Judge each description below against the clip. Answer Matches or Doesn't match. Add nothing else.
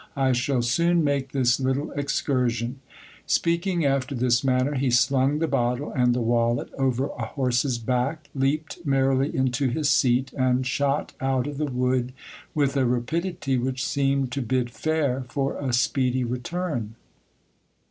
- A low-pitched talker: Matches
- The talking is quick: Doesn't match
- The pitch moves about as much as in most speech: Doesn't match